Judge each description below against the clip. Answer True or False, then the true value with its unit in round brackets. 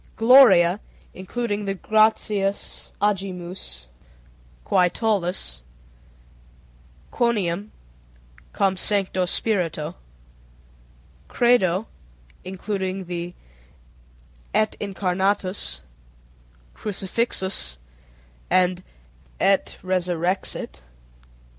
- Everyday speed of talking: False (60 wpm)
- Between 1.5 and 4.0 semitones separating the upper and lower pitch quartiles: True (2.6 semitones)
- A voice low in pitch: False (190 Hz)